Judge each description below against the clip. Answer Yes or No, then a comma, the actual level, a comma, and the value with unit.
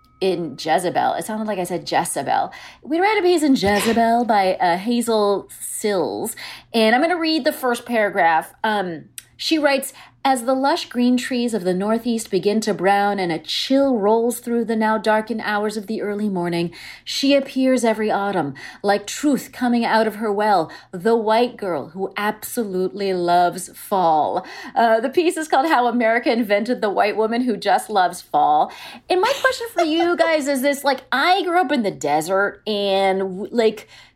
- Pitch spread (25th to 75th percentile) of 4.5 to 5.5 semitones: Yes, average, 5.1 semitones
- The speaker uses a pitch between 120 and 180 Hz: No, high, 225 Hz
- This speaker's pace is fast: No, average, 180 wpm